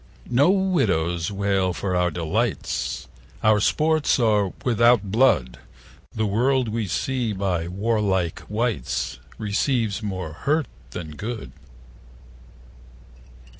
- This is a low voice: Yes, low, 105 Hz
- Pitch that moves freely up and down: No, average, 4.7 semitones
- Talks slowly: Yes, slow, 105 wpm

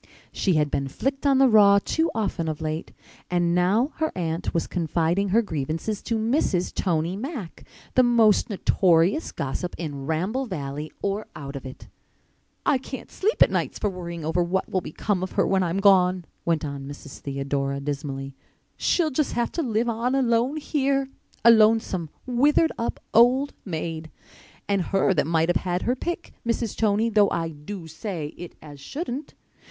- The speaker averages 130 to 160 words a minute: No, average, 170 wpm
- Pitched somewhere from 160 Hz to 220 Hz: Yes, high, 190 Hz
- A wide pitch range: Yes, wide, 6.5 semitones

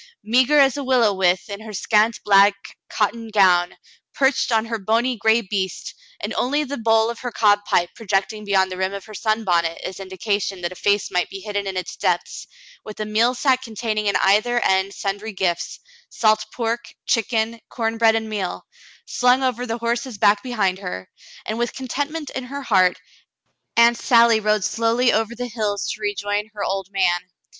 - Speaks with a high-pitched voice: Yes, high, 215 Hz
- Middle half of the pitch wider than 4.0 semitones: No, average, 3.1 semitones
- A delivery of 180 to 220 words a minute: Yes, average, 190 wpm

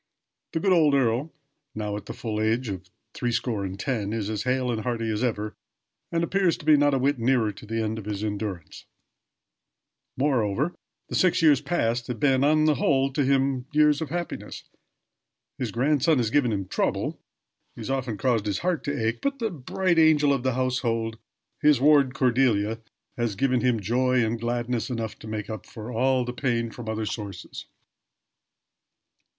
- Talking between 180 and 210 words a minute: Yes, average, 185 wpm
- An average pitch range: Yes, average, 4.2 semitones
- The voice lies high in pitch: No, low, 125 Hz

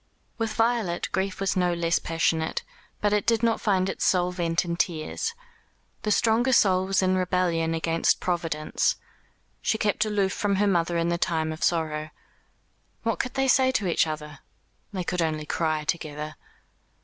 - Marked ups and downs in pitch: No, average, 4.0 semitones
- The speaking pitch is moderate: Yes, medium, 180 Hz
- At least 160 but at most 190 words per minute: Yes, average, 170 wpm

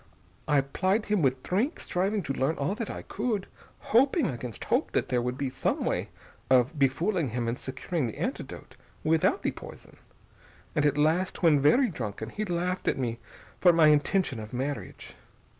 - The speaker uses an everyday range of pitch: No, wide, 6.3 semitones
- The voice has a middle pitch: Yes, medium, 150 Hz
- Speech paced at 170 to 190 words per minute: Yes, average, 175 wpm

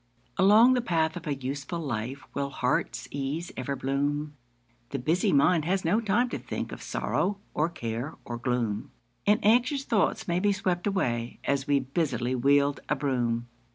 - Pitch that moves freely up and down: Yes, wide, 5.7 semitones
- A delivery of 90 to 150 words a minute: No, average, 170 wpm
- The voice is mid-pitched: Yes, medium, 145 Hz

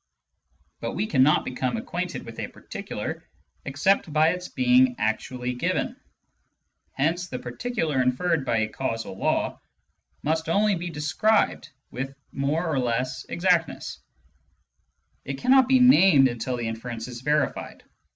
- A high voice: No, medium, 140 Hz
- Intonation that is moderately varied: No, wide, 5.7 semitones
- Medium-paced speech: No, slow, 130 wpm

